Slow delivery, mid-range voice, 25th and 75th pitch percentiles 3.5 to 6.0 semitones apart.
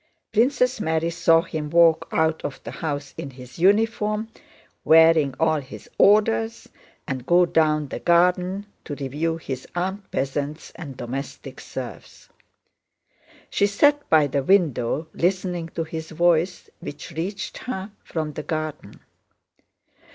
Yes: slow, 130 wpm; medium, 160 Hz; average, 4.0 semitones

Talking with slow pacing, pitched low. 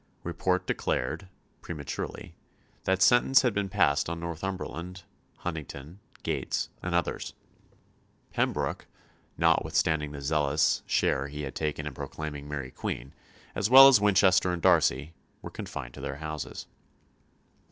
Yes: slow, 125 wpm; very low, 80 Hz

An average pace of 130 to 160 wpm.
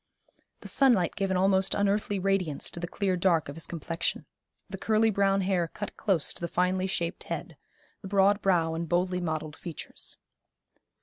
No: average, 175 wpm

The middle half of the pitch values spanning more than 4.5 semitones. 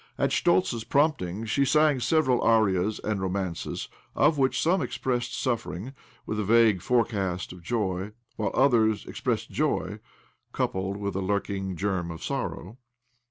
Yes: average, 4.9 semitones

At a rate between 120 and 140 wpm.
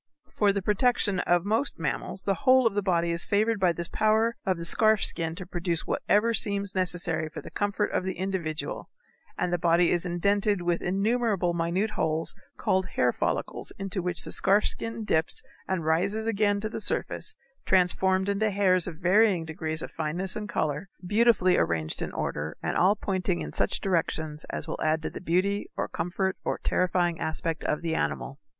No: average, 185 wpm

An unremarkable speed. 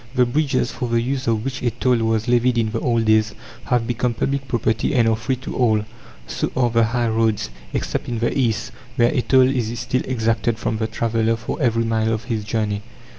No: fast, 220 wpm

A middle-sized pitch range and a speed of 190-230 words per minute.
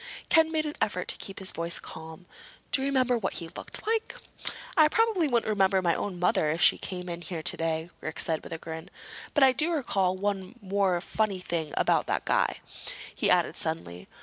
No: wide, 7.2 semitones; average, 200 wpm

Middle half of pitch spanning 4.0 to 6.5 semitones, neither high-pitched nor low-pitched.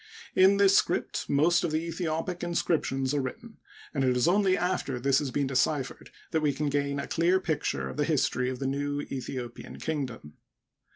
Yes: average, 4.4 semitones; medium, 145 Hz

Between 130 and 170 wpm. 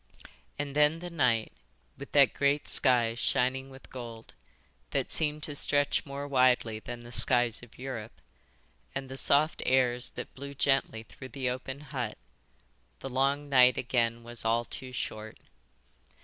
Yes: average, 150 wpm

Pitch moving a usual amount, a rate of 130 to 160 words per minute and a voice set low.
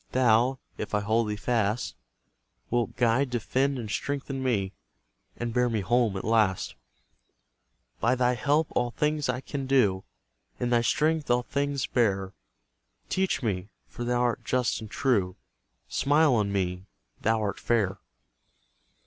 Yes: average, 3.8 semitones; average, 145 wpm; low, 120 Hz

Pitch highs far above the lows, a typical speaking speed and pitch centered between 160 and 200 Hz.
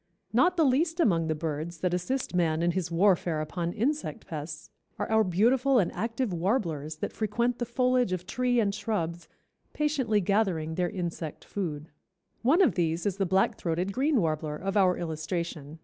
Yes: wide, 6.2 semitones; average, 175 wpm; medium, 185 Hz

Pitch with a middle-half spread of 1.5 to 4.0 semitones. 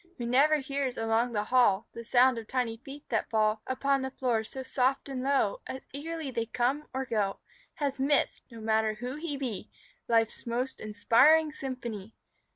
Yes: average, 3.4 semitones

